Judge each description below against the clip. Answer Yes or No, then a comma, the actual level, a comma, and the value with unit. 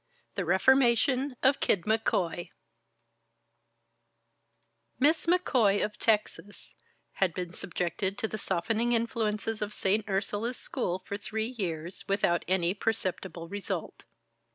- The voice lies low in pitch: No, high, 210 Hz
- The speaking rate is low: Yes, slow, 115 wpm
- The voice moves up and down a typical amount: Yes, average, 3.7 semitones